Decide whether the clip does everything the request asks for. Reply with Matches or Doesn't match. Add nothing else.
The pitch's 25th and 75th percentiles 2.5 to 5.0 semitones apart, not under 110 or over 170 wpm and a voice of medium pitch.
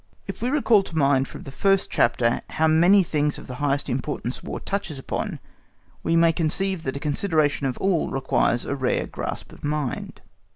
Doesn't match